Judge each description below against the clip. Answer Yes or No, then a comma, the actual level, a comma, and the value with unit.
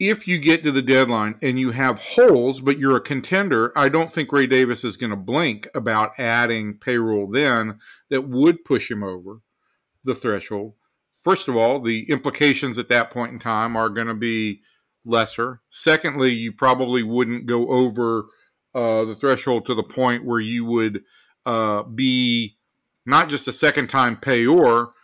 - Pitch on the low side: Yes, low, 120 Hz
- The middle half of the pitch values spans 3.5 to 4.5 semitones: No, average, 2.8 semitones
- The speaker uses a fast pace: No, average, 175 wpm